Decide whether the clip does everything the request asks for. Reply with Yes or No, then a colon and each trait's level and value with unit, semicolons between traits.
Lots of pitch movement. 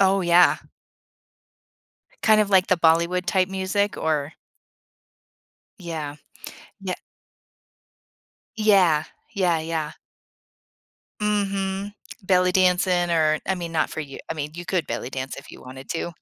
No: average, 3.2 semitones